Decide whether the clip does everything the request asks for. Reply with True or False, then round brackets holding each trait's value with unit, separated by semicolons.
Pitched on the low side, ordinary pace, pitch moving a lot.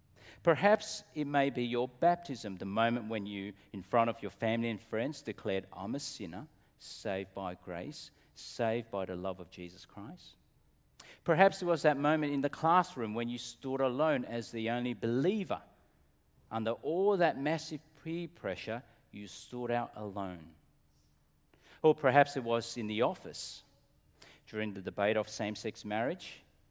True (115 Hz; 155 wpm; 6.2 semitones)